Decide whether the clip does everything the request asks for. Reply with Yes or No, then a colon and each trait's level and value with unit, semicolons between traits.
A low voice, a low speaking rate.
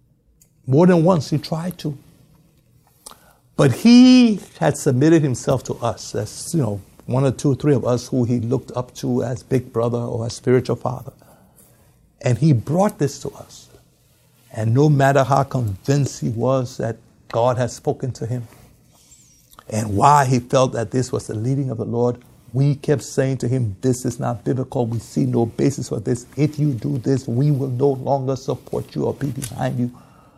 No: low, 130 Hz; average, 190 wpm